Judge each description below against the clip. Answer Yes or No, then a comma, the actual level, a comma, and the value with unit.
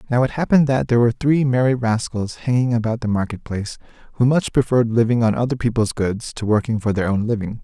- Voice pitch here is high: No, low, 120 Hz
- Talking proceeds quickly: Yes, fast, 220 wpm